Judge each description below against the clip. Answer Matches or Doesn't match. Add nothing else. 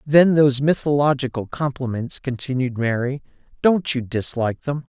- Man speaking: Matches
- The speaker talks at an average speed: Doesn't match